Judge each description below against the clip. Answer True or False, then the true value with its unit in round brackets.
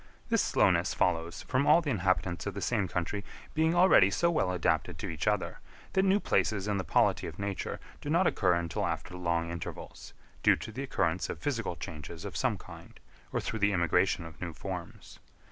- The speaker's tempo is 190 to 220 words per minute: True (195 wpm)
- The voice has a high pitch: False (95 Hz)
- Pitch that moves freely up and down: True (6.7 semitones)